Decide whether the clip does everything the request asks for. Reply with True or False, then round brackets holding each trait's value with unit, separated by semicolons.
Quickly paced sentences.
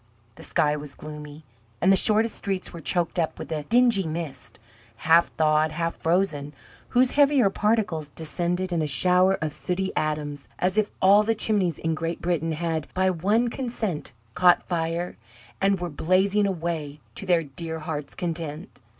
False (165 wpm)